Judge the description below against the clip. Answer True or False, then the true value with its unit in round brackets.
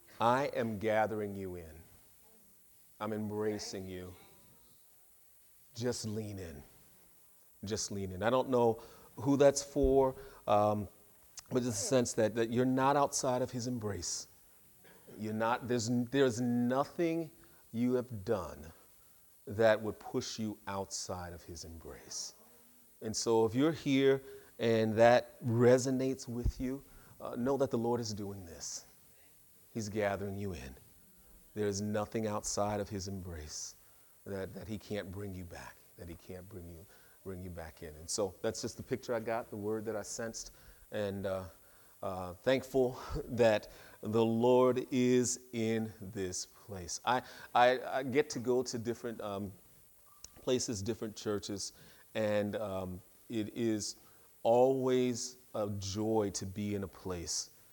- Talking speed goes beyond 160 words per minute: False (150 wpm)